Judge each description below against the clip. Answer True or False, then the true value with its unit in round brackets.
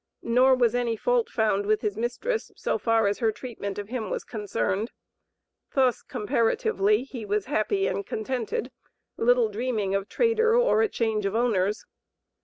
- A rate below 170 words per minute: True (160 wpm)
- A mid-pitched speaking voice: False (225 Hz)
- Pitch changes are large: False (3.5 semitones)